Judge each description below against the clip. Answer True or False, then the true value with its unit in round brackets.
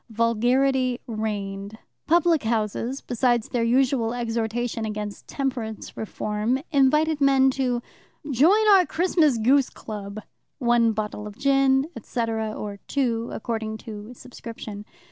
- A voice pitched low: False (235 Hz)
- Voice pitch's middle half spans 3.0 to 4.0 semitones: True (3.6 semitones)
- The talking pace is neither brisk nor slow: False (115 wpm)